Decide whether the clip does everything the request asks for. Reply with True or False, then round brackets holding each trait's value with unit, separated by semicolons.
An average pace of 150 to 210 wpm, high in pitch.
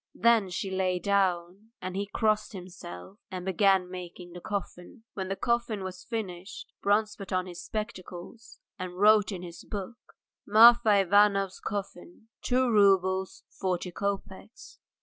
False (140 wpm; 195 Hz)